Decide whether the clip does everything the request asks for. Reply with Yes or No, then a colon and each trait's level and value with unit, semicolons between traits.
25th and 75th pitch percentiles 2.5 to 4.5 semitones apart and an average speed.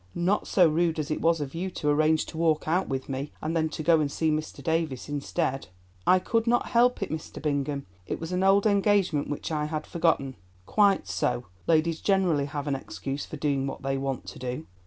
No: average, 3.5 semitones; fast, 220 wpm